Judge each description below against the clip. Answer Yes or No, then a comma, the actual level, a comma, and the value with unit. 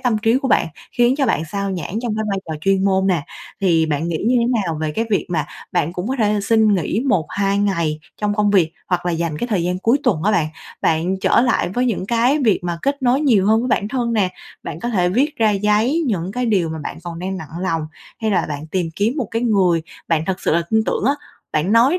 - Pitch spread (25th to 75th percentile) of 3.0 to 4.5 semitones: No, average, 5.1 semitones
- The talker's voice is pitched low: No, high, 200 Hz